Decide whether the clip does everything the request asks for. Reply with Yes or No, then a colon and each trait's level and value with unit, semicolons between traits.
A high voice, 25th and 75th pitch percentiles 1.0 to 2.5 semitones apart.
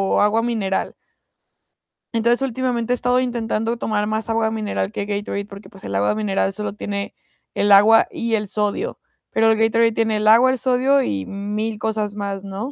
Yes: high, 220 Hz; narrow, 2.2 semitones